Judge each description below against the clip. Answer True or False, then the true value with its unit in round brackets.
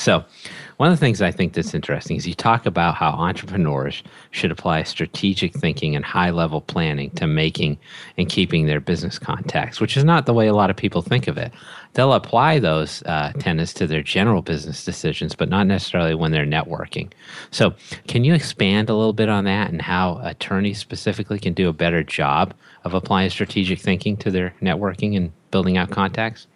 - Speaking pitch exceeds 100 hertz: False (95 Hz)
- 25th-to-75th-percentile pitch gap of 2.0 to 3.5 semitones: False (4.1 semitones)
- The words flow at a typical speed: True (195 wpm)